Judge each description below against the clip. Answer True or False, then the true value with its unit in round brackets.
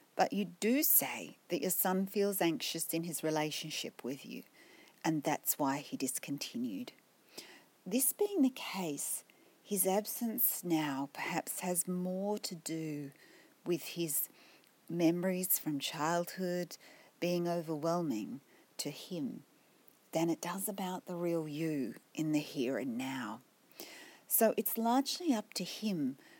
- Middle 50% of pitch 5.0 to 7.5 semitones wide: True (5.3 semitones)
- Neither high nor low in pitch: True (180 Hz)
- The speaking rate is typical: False (130 wpm)